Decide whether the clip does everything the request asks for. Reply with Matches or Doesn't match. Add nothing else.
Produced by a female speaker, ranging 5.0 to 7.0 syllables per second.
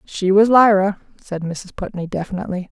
Matches